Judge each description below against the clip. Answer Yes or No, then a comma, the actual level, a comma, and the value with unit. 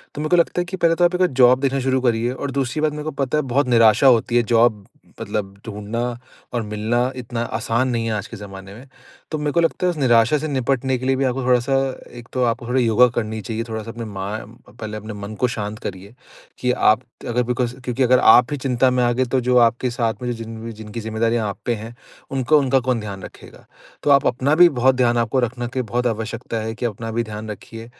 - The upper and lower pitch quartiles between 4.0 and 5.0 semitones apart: No, average, 2.7 semitones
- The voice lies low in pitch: Yes, low, 120 Hz